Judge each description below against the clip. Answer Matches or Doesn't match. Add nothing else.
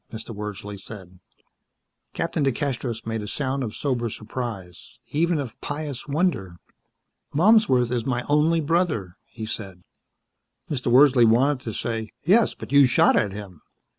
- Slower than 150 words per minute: Matches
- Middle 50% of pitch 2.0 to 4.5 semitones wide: Doesn't match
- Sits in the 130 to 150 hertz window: Doesn't match